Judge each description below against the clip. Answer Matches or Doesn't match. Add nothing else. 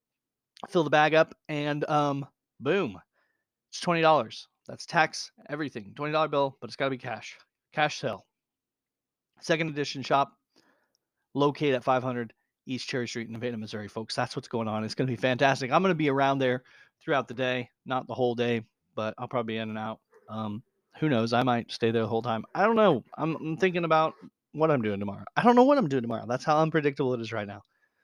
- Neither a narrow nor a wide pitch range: Matches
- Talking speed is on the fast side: Matches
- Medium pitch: Doesn't match